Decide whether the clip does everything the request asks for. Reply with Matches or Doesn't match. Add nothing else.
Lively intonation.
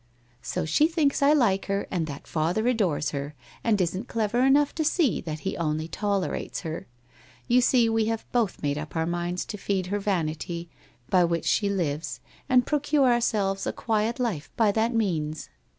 Matches